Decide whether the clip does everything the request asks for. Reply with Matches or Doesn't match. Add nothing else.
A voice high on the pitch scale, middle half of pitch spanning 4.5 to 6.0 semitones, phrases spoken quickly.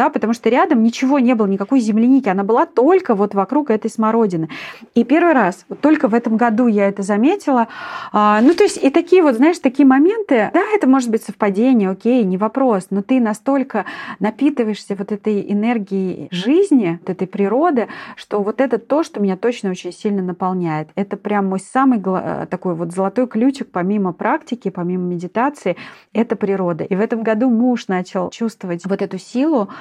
Matches